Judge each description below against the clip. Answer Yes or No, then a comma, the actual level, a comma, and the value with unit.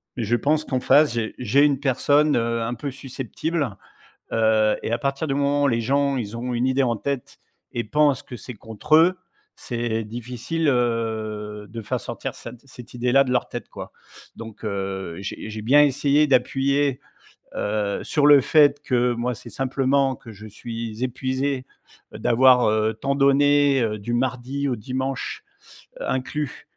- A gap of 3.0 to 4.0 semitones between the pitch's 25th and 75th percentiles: Yes, average, 3.5 semitones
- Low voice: Yes, low, 125 Hz